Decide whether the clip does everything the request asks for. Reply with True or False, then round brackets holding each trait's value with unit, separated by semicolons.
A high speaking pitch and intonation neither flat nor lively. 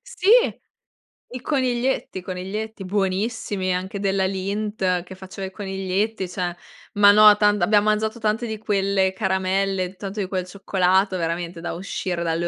False (195 Hz; 2.2 semitones)